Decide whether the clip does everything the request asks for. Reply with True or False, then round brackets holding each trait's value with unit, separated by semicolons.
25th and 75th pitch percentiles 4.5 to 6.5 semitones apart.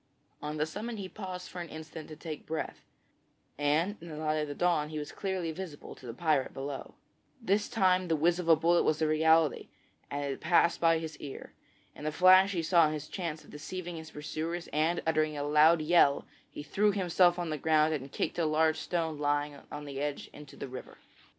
False (2.7 semitones)